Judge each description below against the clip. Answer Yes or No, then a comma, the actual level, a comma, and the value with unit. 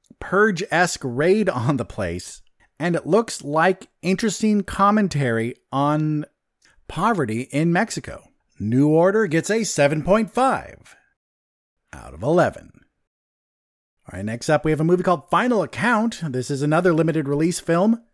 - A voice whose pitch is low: No, medium, 165 Hz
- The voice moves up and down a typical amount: No, wide, 5.8 semitones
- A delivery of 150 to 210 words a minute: No, slow, 135 wpm